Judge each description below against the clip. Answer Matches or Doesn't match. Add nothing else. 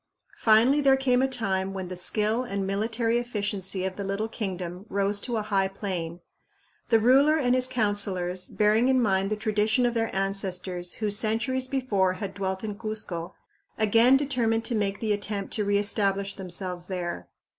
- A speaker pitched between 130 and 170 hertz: Doesn't match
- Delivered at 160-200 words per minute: Matches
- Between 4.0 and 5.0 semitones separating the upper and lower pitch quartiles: Doesn't match